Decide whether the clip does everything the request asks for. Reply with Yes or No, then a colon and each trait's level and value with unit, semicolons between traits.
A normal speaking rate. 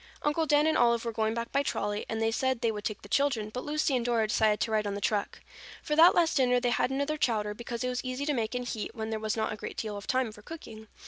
No: fast, 300 wpm